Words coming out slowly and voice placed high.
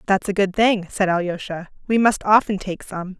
No: fast, 205 wpm; high, 195 Hz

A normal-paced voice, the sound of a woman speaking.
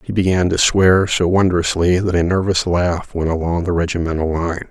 No: average, 190 wpm; male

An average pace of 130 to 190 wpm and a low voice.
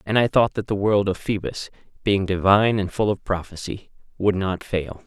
No: average, 200 wpm; low, 100 Hz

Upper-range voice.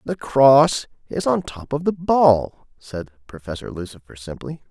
No: low, 130 Hz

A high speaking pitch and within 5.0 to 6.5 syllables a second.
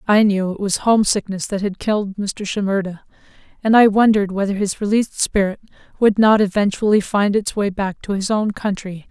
Yes: high, 200 Hz; 5.6 syllables/s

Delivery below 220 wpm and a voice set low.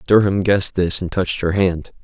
Yes: fast, 205 wpm; very low, 95 Hz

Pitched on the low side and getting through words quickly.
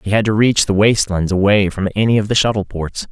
Yes: low, 100 Hz; fast, 250 wpm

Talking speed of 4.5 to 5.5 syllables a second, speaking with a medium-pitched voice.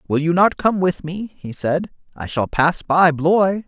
No: 4.1 syllables/s; medium, 170 Hz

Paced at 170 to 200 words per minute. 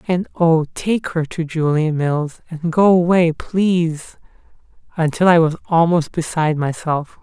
No: average, 140 wpm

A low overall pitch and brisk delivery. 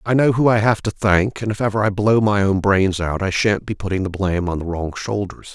Yes: low, 100 Hz; fast, 280 wpm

